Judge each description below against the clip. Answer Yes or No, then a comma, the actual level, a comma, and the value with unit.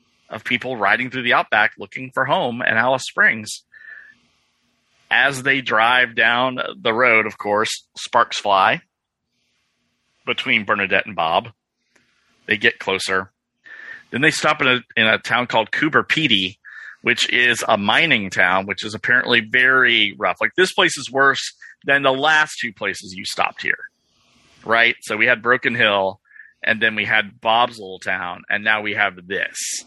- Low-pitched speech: Yes, low, 120 Hz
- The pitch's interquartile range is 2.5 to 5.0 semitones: Yes, average, 4.5 semitones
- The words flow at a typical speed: Yes, average, 165 wpm